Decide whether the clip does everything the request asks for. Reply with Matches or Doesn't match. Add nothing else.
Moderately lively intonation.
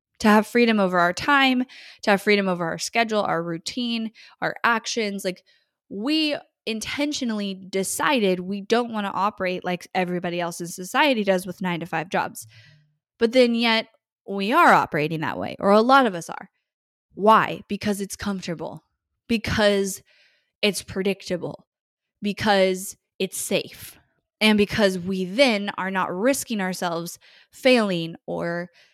Matches